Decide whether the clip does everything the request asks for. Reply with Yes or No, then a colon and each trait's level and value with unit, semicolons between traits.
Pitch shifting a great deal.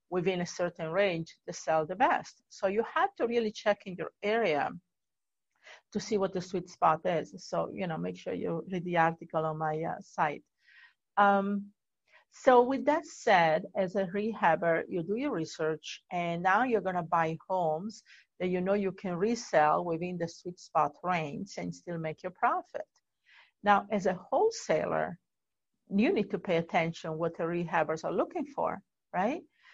No: average, 4.0 semitones